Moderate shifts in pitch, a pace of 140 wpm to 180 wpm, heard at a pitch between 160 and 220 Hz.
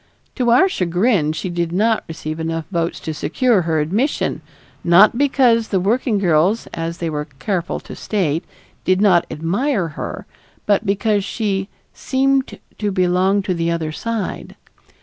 Yes: average, 4.9 semitones; average, 150 wpm; high, 190 Hz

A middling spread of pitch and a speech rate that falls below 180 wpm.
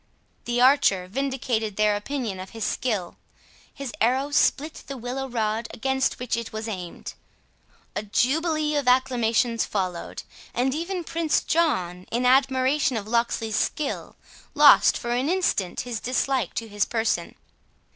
Yes: average, 3.9 semitones; average, 140 wpm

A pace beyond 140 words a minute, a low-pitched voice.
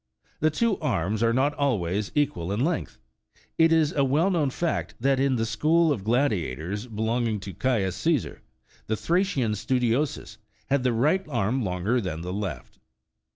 Yes: average, 165 wpm; low, 120 Hz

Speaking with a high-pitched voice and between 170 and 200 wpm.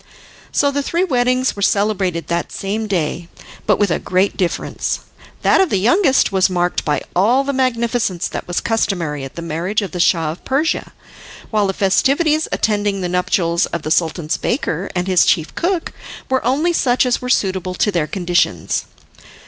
Yes: high, 195 Hz; average, 180 wpm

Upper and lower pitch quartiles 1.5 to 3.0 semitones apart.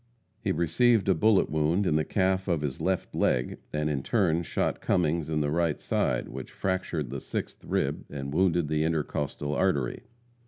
No: average, 3.8 semitones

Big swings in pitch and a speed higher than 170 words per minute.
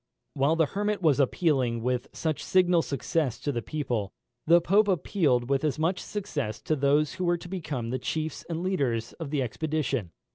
No: average, 4.8 semitones; average, 185 wpm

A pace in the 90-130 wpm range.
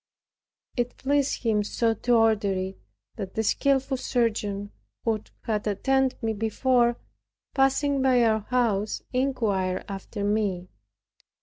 Yes: slow, 120 wpm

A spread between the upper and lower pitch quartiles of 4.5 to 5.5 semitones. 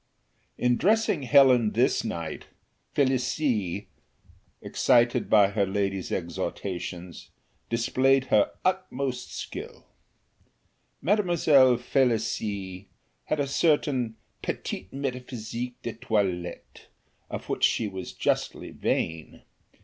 Yes: average, 5.2 semitones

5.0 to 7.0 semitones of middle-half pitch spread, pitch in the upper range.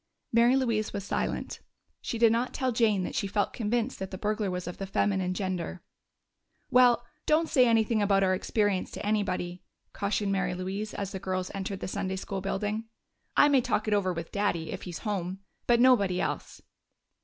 No: average, 3.3 semitones; high, 200 Hz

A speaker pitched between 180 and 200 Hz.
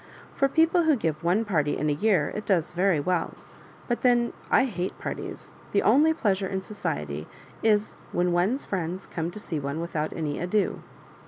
Yes: medium, 185 Hz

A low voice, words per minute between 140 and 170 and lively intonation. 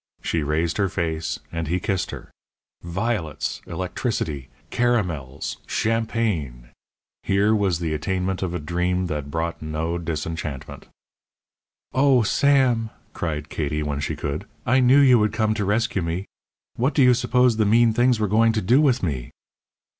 Yes: very low, 95 Hz; average, 155 wpm; wide, 6.3 semitones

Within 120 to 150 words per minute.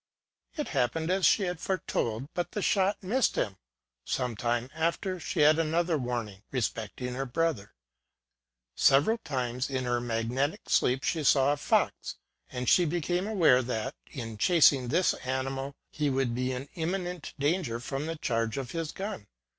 No: average, 160 wpm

